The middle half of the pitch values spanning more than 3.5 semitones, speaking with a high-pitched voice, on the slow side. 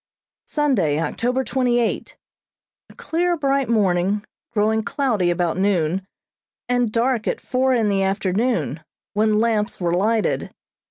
Yes: average, 4.6 semitones; high, 220 Hz; slow, 125 wpm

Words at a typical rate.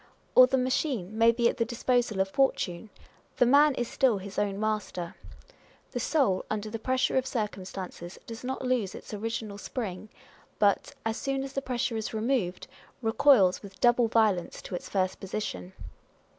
Yes: average, 170 wpm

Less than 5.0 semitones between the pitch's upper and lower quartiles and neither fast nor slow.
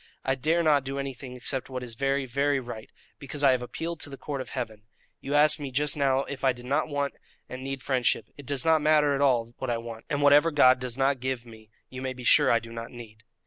No: narrow, 2.5 semitones; fast, 255 wpm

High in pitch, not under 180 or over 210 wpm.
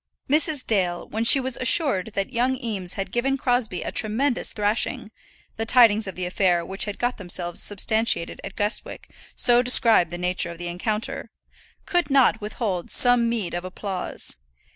No: high, 215 Hz; average, 165 wpm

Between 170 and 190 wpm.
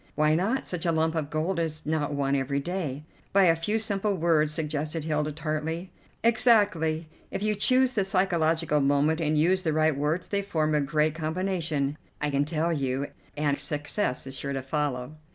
Yes: average, 185 wpm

